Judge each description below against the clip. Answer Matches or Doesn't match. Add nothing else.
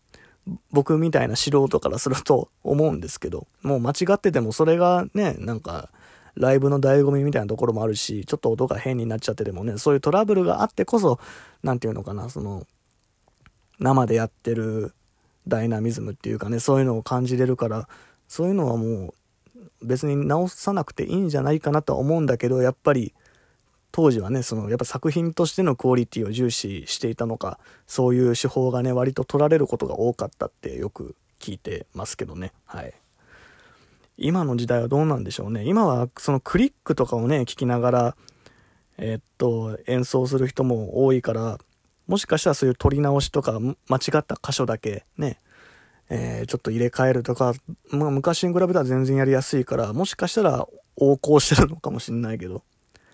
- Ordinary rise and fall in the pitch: Matches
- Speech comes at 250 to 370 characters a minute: Doesn't match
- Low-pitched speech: Matches